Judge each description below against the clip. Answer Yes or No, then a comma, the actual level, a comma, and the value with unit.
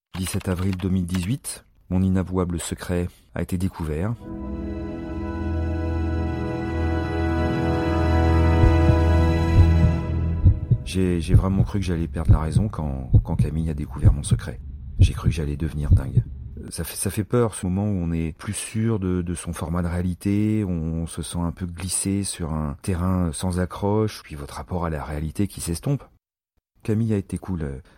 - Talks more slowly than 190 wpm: Yes, average, 155 wpm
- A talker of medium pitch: No, very low, 85 Hz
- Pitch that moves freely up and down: No, average, 2.8 semitones